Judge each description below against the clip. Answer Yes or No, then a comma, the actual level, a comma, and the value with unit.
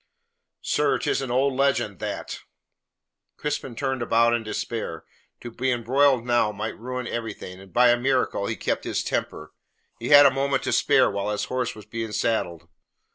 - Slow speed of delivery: No, average, 175 wpm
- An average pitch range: Yes, average, 3.4 semitones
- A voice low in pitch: Yes, low, 120 Hz